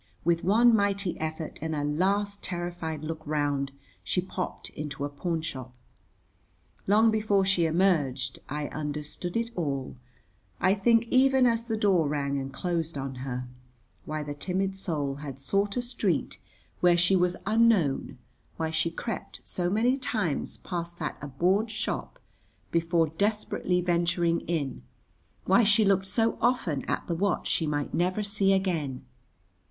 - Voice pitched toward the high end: No, medium, 175 Hz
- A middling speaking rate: Yes, average, 145 wpm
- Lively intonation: No, average, 5.0 semitones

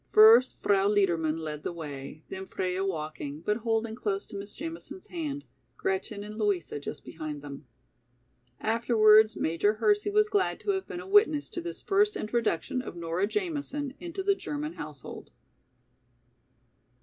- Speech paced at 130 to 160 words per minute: Yes, average, 150 wpm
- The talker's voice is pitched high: Yes, high, 215 Hz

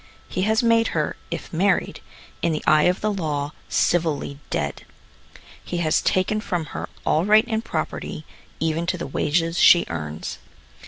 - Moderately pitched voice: Yes, medium, 170 Hz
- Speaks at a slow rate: No, average, 160 wpm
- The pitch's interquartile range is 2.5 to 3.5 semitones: No, average, 4.6 semitones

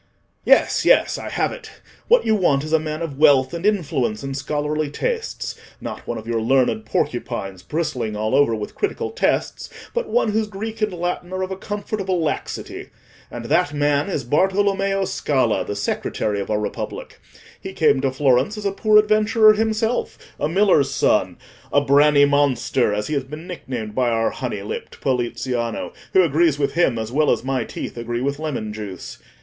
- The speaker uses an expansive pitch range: Yes, wide, 7.5 semitones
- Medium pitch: Yes, medium, 145 Hz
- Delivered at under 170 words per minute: No, average, 175 wpm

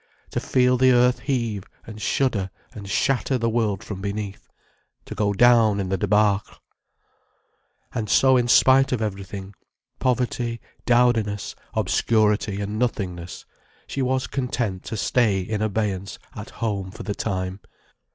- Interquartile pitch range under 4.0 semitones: Yes, average, 3.6 semitones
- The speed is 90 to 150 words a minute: Yes, average, 140 wpm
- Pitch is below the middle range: Yes, low, 110 Hz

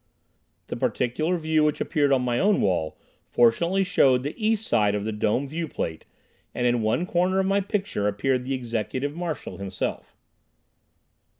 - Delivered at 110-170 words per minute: Yes, average, 160 wpm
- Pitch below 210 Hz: Yes, low, 135 Hz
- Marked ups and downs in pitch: Yes, wide, 7.4 semitones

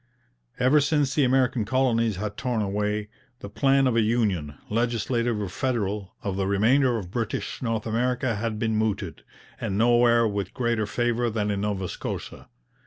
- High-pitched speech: No, low, 115 Hz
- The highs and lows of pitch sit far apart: No, average, 2.9 semitones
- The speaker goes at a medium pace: Yes, average, 165 wpm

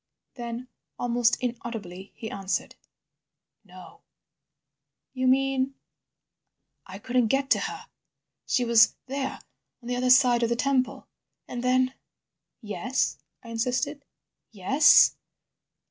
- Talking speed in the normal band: No, slow, 110 wpm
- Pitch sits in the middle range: No, high, 245 Hz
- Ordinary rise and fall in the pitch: No, narrow, 2.2 semitones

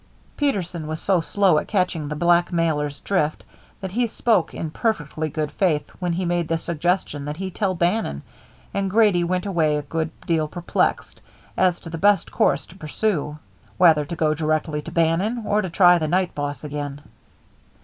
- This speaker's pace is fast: No, average, 180 wpm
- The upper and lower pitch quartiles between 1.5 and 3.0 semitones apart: No, average, 3.5 semitones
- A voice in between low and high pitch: Yes, medium, 170 Hz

